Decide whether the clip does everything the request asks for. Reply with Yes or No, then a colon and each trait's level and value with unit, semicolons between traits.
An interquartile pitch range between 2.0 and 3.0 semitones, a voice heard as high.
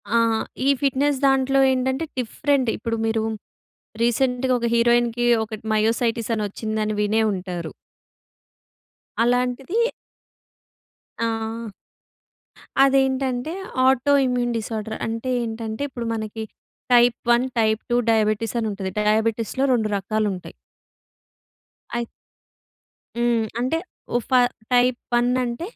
Yes: narrow, 2.4 semitones; high, 235 Hz